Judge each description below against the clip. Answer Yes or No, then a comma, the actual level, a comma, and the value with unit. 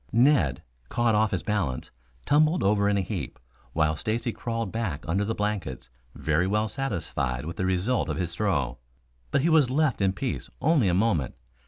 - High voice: No, low, 100 Hz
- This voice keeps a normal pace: Yes, average, 180 wpm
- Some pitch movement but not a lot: No, wide, 5.8 semitones